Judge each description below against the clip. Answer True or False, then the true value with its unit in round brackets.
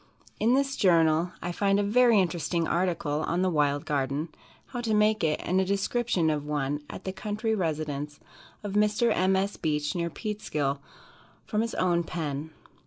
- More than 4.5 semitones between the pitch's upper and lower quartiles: True (5.5 semitones)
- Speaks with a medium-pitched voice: True (175 Hz)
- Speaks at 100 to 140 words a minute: False (175 wpm)